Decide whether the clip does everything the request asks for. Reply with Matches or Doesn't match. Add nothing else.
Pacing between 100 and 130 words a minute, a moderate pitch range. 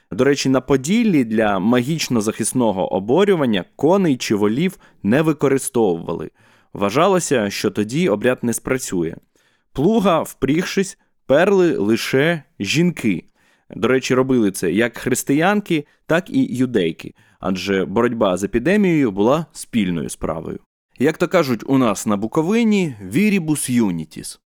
Doesn't match